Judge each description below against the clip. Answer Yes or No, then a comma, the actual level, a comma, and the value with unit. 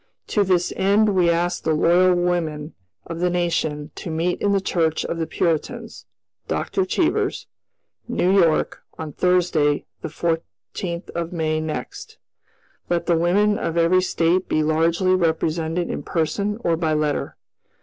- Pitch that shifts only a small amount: Yes, narrow, 2.3 semitones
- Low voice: No, medium, 170 Hz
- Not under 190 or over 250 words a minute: No, average, 150 wpm